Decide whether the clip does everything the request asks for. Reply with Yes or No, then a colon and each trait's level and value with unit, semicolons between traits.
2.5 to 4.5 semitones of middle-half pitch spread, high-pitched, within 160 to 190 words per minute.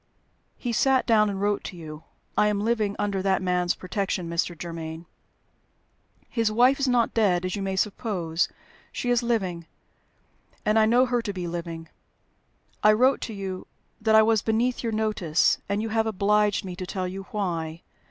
Yes: average, 3.7 semitones; high, 205 Hz; average, 180 wpm